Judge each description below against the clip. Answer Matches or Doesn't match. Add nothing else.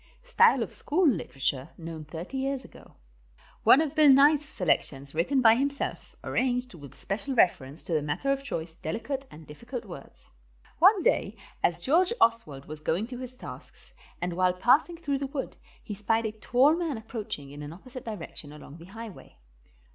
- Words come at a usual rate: Matches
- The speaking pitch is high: Matches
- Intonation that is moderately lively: Doesn't match